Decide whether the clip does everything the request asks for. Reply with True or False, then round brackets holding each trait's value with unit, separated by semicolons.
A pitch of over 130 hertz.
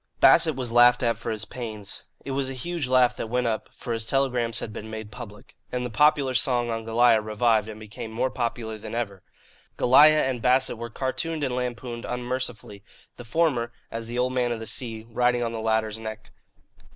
False (120 Hz)